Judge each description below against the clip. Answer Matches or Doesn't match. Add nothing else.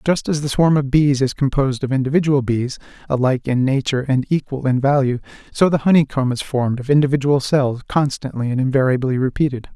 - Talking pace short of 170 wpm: Doesn't match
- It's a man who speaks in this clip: Matches